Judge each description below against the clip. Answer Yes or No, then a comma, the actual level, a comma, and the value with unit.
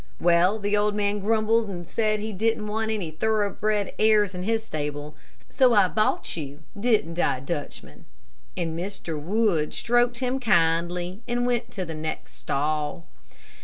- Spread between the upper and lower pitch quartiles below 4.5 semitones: No, average, 4.8 semitones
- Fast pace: No, average, 155 wpm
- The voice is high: Yes, high, 200 Hz